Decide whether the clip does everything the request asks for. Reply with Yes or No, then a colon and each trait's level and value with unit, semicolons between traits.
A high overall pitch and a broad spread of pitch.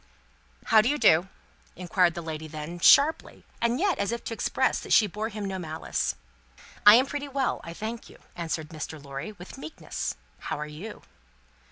Yes: high, 195 Hz; wide, 6.6 semitones